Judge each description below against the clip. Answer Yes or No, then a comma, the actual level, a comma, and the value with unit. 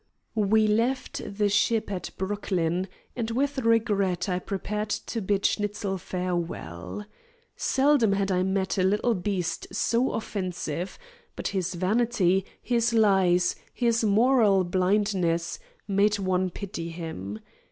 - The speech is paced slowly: Yes, slow, 120 wpm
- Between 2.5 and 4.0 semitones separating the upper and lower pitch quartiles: Yes, average, 3.3 semitones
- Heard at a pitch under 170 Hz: No, high, 200 Hz